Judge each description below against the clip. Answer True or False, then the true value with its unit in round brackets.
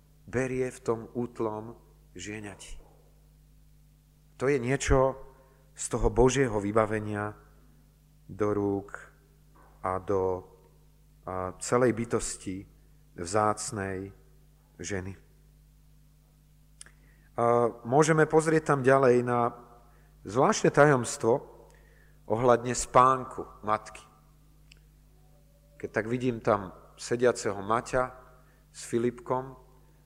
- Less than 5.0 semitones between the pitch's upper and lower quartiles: False (6.2 semitones)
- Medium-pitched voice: False (125 Hz)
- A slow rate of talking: True (80 wpm)